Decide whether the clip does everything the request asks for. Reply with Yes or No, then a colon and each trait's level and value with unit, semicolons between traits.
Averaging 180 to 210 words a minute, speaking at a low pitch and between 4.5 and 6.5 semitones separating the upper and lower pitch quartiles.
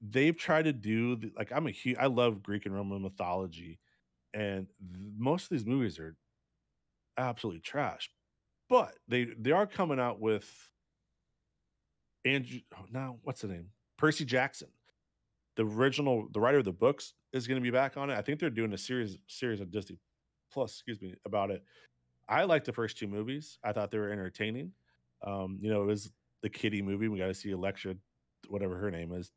Yes: average, 190 wpm; low, 105 Hz; average, 5.0 semitones